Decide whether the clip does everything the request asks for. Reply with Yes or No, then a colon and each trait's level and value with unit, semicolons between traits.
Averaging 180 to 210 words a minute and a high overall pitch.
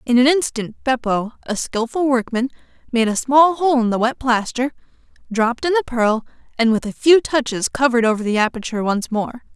Yes: average, 190 wpm; high, 245 Hz